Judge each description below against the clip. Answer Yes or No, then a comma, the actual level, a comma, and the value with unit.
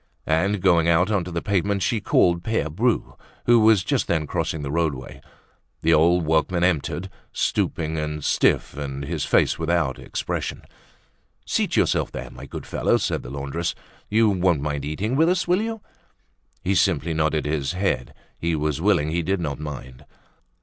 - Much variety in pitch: No, average, 4.3 semitones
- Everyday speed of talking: Yes, average, 170 wpm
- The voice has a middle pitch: No, very low, 85 Hz